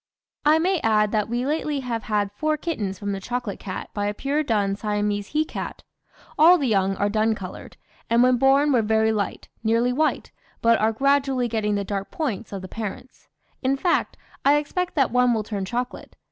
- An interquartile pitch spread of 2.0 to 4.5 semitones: No, average, 4.9 semitones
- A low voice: No, high, 230 Hz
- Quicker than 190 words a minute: Yes, average, 200 wpm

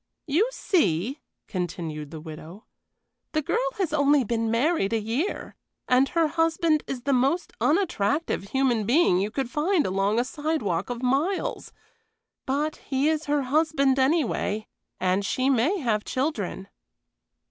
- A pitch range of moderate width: No, wide, 6.6 semitones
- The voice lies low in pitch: No, very high, 265 Hz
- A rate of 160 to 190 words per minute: No, average, 140 wpm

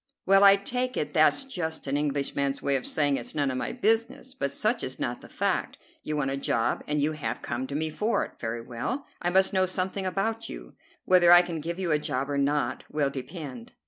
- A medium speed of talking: No, fast, 230 wpm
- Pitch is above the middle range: No, medium, 155 Hz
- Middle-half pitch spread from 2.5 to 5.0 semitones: No, wide, 5.6 semitones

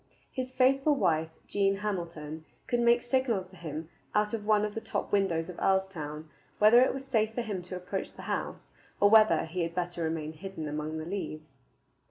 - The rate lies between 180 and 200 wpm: Yes, average, 195 wpm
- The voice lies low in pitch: No, high, 190 Hz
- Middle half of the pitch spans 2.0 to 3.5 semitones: No, average, 5.1 semitones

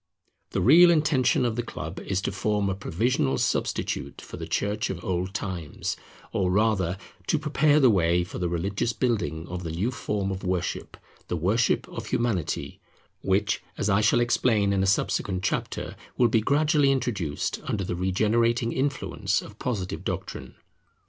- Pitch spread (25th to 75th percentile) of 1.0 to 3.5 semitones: No, average, 4.6 semitones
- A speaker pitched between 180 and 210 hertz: No, low, 105 Hz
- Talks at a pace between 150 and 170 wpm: Yes, average, 165 wpm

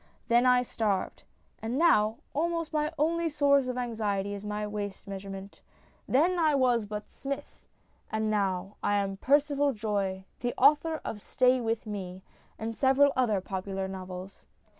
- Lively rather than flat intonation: Yes, wide, 5.7 semitones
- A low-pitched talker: No, high, 225 Hz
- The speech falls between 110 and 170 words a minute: Yes, average, 150 wpm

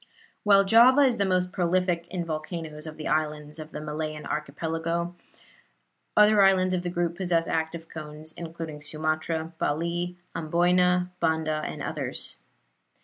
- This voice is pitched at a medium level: Yes, medium, 165 Hz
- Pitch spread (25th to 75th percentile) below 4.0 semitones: Yes, narrow, 2.5 semitones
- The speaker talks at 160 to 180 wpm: No, average, 140 wpm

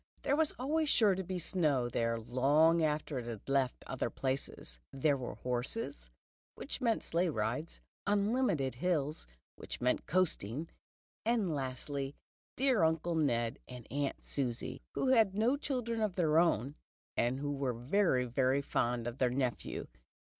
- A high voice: No, medium, 145 Hz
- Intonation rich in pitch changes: Yes, wide, 7.0 semitones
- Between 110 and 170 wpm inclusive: Yes, average, 150 wpm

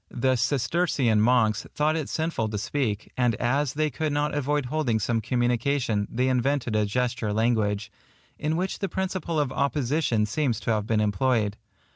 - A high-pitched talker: No, low, 125 Hz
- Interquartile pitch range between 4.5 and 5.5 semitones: Yes, average, 4.9 semitones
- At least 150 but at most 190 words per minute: Yes, average, 165 wpm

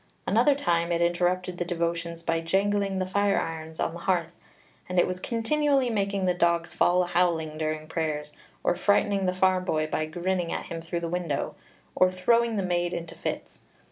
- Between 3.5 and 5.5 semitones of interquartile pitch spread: No, narrow, 2.4 semitones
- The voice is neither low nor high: Yes, medium, 175 Hz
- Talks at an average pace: Yes, average, 190 wpm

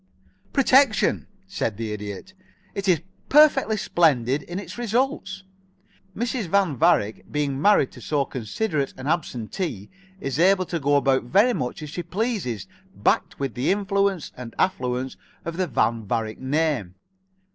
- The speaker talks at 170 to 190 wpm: No, average, 145 wpm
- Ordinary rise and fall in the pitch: No, wide, 7.8 semitones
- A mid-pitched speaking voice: Yes, medium, 155 Hz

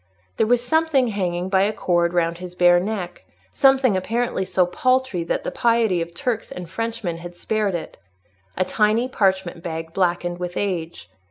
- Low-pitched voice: No, medium, 185 Hz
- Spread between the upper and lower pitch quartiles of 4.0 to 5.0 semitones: Yes, average, 4.4 semitones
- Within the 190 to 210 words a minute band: No, average, 165 wpm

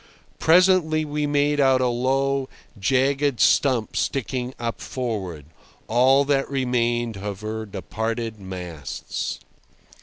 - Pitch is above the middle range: No, low, 125 Hz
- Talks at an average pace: No, slow, 100 wpm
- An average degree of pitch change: Yes, average, 4.0 semitones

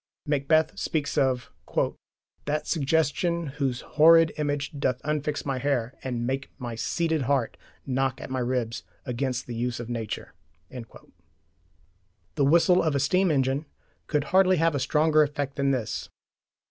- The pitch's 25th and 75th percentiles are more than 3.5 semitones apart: No, average, 3.2 semitones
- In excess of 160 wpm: No, average, 145 wpm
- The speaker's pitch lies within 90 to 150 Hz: Yes, medium, 140 Hz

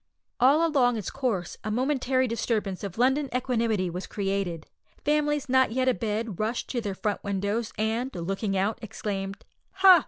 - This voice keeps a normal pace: Yes, average, 155 wpm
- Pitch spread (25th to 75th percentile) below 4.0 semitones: No, average, 4.6 semitones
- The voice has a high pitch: Yes, high, 225 Hz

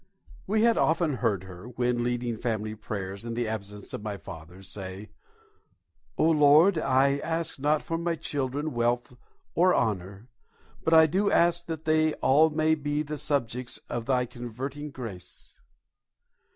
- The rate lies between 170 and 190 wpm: No, average, 150 wpm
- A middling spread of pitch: No, wide, 6.1 semitones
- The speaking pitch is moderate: No, low, 130 Hz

